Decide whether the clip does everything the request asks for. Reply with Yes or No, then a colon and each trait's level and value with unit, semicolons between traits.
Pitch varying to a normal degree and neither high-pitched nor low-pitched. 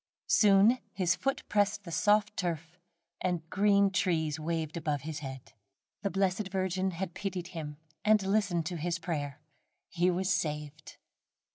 Yes: average, 3.6 semitones; medium, 180 Hz